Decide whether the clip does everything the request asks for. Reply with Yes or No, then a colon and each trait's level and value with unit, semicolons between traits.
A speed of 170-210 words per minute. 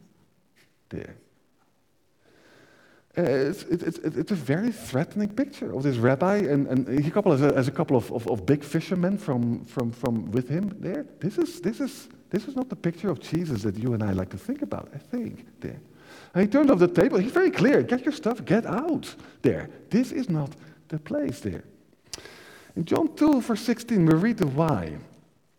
Yes: average, 195 wpm